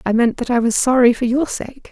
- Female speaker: Yes, female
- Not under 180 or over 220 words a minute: No, fast, 280 wpm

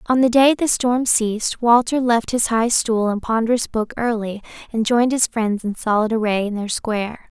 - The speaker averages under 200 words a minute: No, fast, 205 wpm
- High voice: Yes, high, 230 Hz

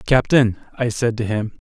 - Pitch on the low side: Yes, low, 120 Hz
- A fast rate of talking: No, average, 180 wpm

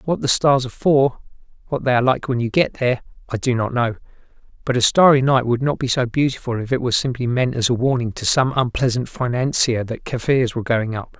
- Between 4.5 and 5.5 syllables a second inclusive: No, 6.0 syllables/s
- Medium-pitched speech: No, low, 125 Hz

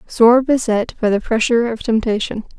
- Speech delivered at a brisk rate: No, average, 165 wpm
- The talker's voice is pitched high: Yes, high, 230 Hz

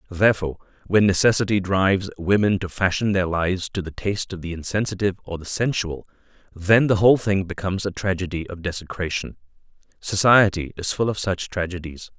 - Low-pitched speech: Yes, very low, 95 Hz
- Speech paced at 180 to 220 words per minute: No, average, 160 wpm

